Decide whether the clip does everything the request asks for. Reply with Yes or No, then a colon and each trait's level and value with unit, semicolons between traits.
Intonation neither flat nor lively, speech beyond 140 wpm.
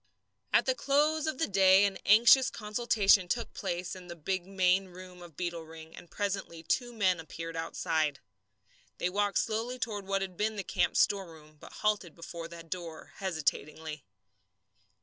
Yes: average, 3.9 semitones; average, 165 wpm